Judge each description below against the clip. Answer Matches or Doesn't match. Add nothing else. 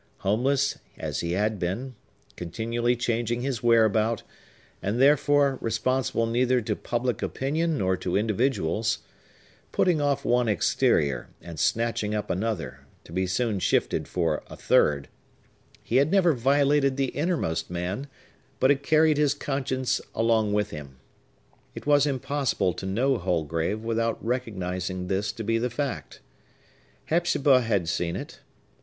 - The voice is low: Matches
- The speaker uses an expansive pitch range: Matches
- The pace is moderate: Doesn't match